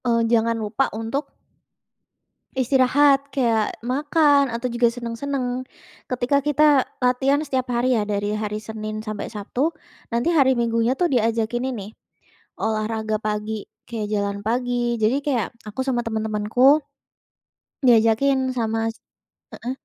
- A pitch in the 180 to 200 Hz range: No, high, 235 Hz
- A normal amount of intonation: Yes, average, 3.2 semitones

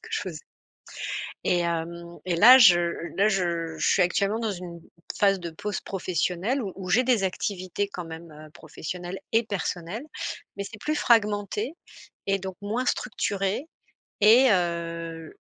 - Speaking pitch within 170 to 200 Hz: Yes, high, 190 Hz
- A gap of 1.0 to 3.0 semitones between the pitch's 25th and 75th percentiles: No, average, 3.7 semitones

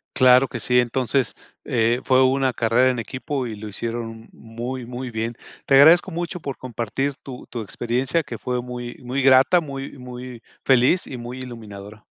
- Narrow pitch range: Yes, narrow, 2.3 semitones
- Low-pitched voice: Yes, low, 125 Hz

